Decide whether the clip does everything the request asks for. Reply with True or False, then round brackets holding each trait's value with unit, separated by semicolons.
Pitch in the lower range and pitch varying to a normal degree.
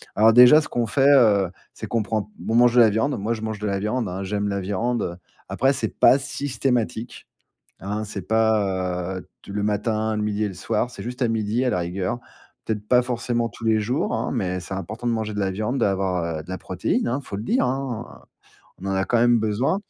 True (110 Hz; 3.4 semitones)